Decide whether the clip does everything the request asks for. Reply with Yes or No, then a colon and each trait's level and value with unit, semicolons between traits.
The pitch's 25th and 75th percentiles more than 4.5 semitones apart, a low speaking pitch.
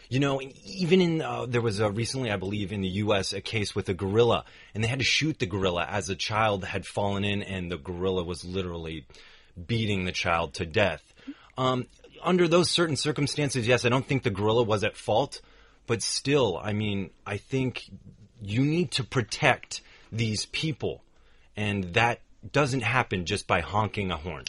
Yes: average, 5.1 semitones; low, 105 Hz